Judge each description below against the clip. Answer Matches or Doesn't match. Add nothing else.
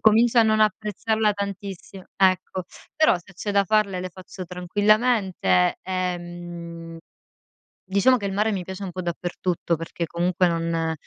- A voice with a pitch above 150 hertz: Matches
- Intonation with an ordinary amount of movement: Matches